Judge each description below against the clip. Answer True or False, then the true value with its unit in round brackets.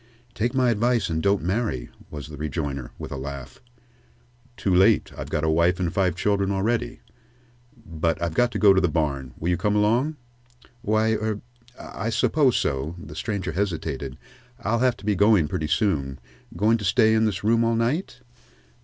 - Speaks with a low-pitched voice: True (100 Hz)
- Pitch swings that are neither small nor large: False (6.0 semitones)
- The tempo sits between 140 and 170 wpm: False (180 wpm)